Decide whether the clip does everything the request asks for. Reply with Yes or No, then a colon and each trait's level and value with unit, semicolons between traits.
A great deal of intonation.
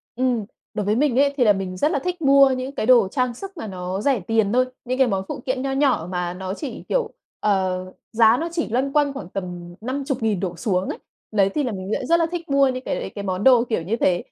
Yes: wide, 6.1 semitones